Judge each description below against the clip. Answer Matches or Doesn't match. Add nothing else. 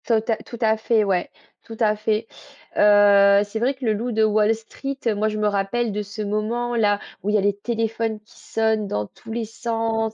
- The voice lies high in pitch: Matches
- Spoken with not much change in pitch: Matches